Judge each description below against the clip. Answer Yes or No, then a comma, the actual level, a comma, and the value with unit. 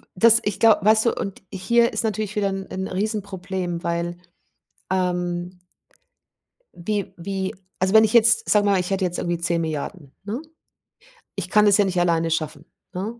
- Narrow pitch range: No, average, 3.1 semitones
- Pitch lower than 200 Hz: Yes, high, 190 Hz